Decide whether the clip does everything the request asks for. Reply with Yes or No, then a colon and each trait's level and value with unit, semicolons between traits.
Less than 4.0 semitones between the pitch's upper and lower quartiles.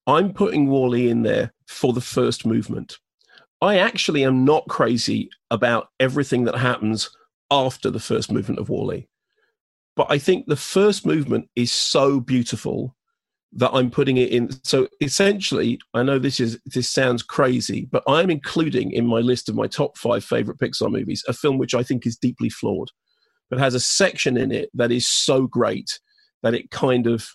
Yes: average, 3.3 semitones